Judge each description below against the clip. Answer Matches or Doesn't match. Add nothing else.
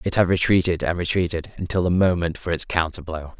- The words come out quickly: Matches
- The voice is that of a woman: Doesn't match